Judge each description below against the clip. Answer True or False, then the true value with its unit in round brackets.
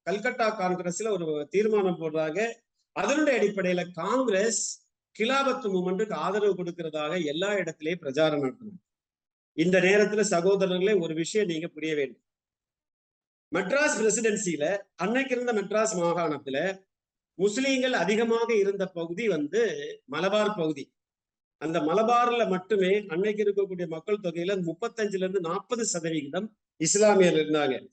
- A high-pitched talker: True (195 Hz)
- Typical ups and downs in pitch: True (4.5 semitones)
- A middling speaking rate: True (105 wpm)